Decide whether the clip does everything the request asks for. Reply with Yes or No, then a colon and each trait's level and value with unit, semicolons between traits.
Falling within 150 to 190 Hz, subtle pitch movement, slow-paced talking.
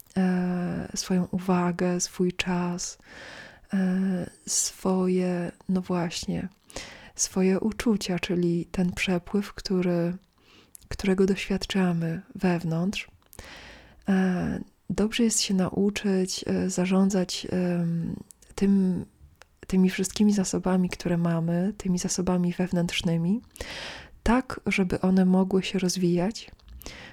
Yes: medium, 185 Hz; narrow, 1.5 semitones; slow, 75 wpm